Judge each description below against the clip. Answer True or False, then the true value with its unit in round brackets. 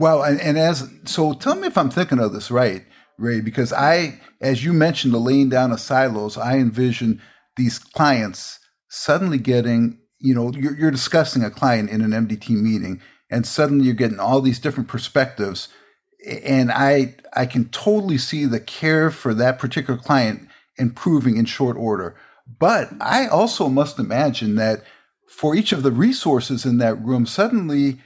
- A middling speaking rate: True (165 wpm)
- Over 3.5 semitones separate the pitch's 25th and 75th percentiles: True (4.1 semitones)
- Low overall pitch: True (130 Hz)